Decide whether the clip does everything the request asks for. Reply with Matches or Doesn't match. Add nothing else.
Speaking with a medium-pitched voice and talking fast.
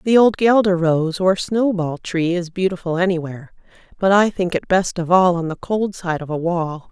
Matches